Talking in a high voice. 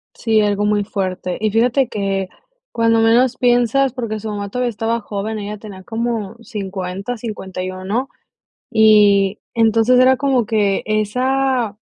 Yes: high, 220 Hz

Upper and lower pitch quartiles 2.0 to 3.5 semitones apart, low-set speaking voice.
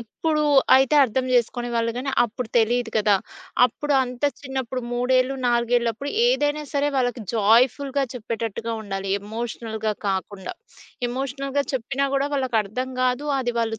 No: average, 2.9 semitones; high, 245 Hz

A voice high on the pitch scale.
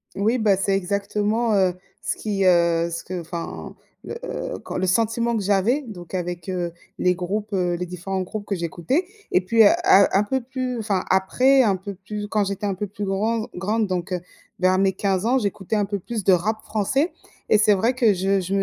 Yes: high, 200 Hz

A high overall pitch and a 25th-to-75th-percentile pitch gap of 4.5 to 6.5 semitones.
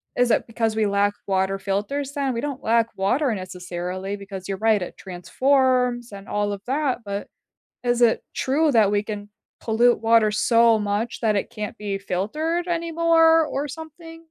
Yes: high, 225 Hz; average, 5.3 semitones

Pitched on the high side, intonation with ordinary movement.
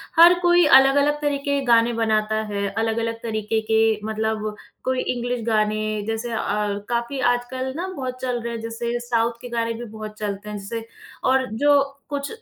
Yes: high, 230 Hz; average, 3.0 semitones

